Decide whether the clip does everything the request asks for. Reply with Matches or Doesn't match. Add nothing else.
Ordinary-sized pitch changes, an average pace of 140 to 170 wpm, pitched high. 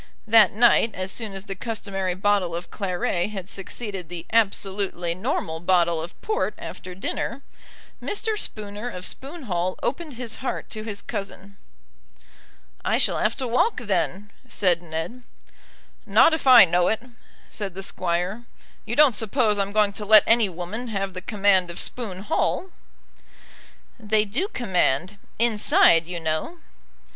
Matches